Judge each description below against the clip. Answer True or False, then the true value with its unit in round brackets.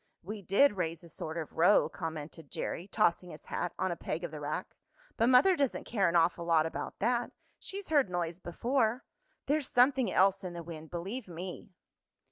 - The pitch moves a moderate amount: False (6.1 semitones)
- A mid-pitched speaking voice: True (180 Hz)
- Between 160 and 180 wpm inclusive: False (190 wpm)